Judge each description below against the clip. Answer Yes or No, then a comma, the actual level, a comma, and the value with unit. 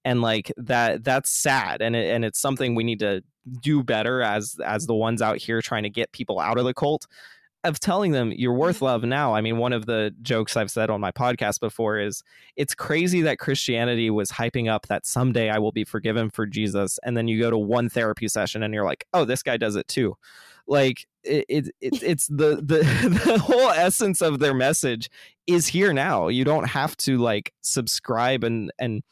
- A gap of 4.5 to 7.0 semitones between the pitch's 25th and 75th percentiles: No, average, 3.8 semitones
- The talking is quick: Yes, fast, 215 wpm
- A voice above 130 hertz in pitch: No, low, 120 Hz